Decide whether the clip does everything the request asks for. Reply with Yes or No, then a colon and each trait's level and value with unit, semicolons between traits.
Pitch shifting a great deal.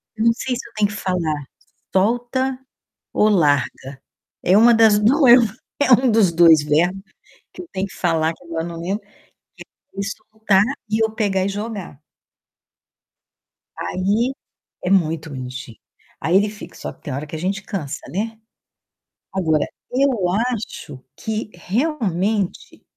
No: average, 5.0 semitones